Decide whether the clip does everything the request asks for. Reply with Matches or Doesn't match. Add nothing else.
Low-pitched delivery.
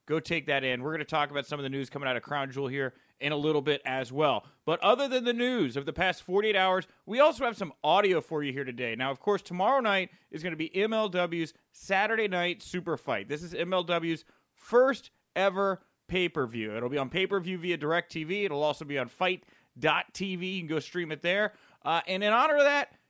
Doesn't match